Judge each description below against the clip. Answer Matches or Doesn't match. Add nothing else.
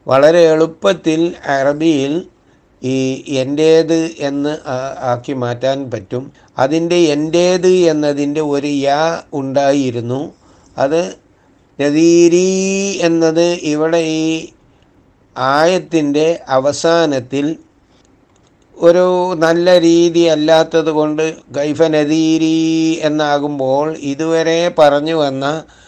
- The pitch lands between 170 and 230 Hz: Doesn't match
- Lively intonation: Doesn't match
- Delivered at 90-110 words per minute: Doesn't match